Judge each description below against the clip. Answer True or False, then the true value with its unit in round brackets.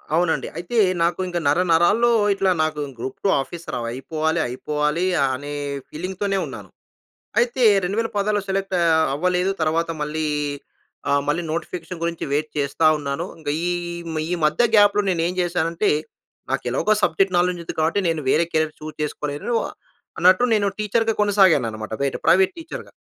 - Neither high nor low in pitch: True (170 Hz)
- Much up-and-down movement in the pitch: False (4.0 semitones)